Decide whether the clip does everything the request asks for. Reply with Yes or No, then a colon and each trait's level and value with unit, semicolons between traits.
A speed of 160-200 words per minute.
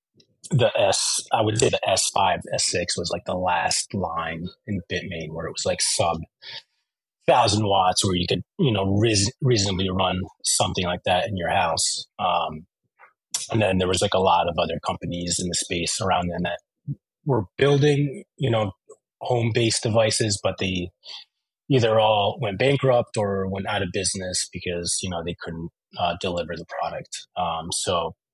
Yes: average, 175 wpm